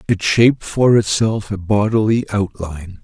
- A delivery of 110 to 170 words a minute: Yes, average, 140 wpm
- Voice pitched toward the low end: Yes, low, 105 Hz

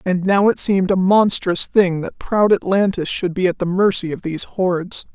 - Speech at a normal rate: No, fast, 210 wpm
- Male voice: No, female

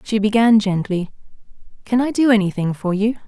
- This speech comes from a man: No, female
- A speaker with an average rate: Yes, average, 165 wpm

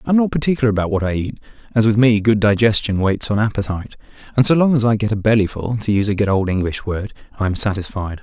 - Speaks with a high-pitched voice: No, low, 110 Hz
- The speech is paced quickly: Yes, fast, 235 wpm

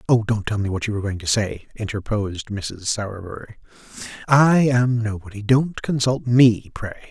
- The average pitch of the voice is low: Yes, low, 110 Hz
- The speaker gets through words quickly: No, average, 170 wpm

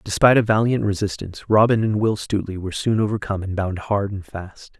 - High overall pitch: No, low, 100 Hz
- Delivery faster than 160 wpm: Yes, average, 200 wpm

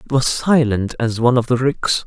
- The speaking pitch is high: No, low, 125 Hz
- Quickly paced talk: Yes, fast, 235 wpm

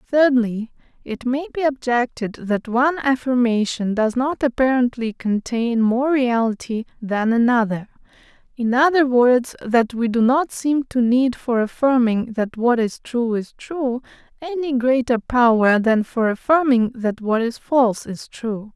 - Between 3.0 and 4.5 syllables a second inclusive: Yes, 4.2 syllables/s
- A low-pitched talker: No, high, 245 Hz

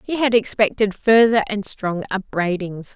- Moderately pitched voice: No, high, 205 Hz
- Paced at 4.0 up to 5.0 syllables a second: Yes, 4.5 syllables/s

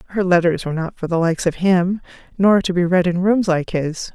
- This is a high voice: No, medium, 180 Hz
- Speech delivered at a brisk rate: Yes, fast, 245 wpm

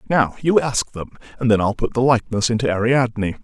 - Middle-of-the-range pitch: No, low, 115 Hz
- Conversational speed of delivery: No, fast, 210 wpm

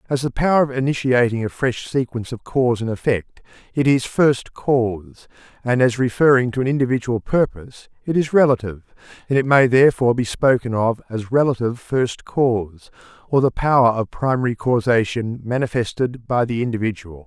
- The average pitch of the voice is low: Yes, low, 120 Hz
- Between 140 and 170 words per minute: Yes, average, 165 wpm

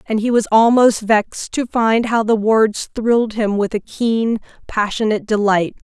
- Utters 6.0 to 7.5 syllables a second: No, 4.5 syllables/s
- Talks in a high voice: Yes, high, 220 Hz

